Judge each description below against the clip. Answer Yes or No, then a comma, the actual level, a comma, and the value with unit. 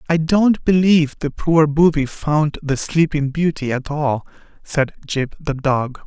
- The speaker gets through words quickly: No, average, 160 wpm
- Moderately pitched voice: Yes, medium, 150 Hz